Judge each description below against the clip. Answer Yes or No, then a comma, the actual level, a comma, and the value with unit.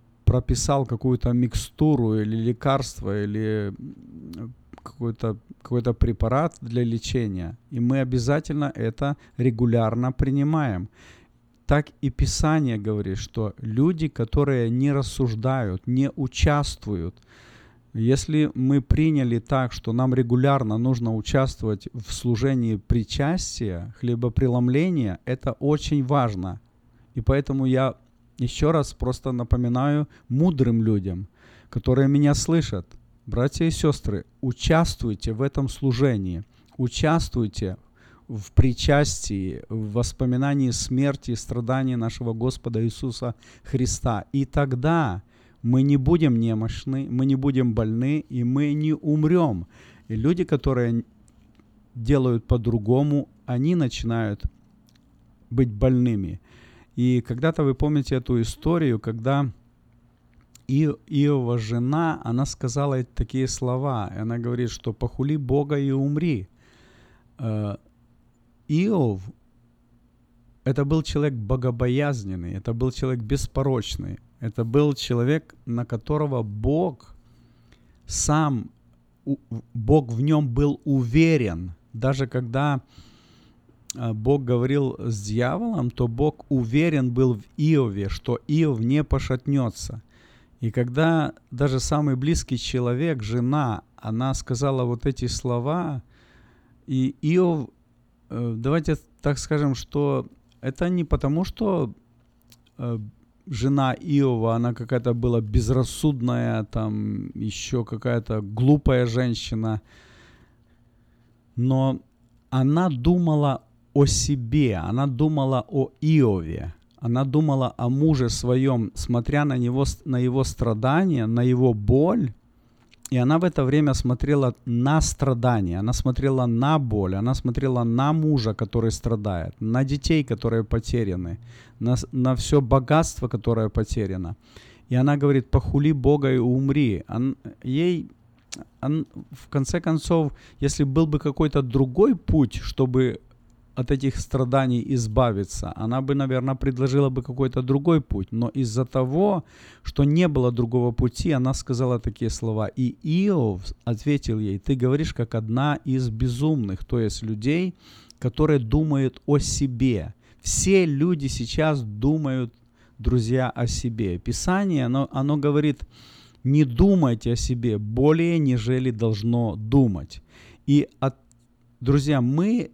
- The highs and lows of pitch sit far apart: No, average, 3.4 semitones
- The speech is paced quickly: No, average, 115 wpm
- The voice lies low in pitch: Yes, low, 125 Hz